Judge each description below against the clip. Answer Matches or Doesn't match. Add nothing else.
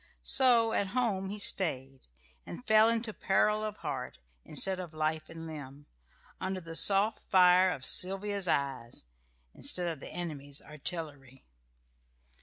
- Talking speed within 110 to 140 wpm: Matches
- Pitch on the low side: Doesn't match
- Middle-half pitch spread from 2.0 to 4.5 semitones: Doesn't match